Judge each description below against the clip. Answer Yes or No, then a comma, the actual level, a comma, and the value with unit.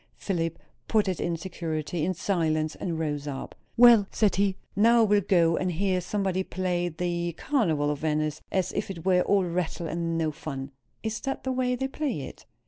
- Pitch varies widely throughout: No, average, 3.9 semitones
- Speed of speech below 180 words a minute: No, average, 195 wpm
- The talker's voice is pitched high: No, medium, 175 Hz